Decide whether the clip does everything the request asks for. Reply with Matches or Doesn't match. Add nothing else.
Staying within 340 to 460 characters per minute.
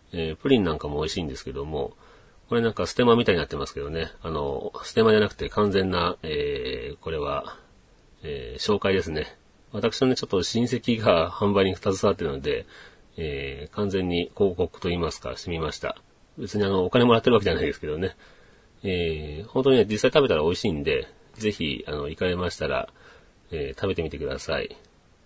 Matches